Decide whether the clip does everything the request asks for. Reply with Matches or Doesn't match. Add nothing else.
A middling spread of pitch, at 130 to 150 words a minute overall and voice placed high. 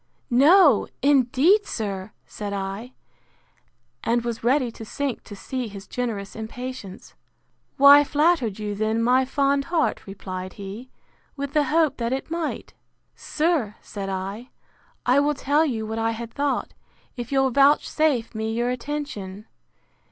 Matches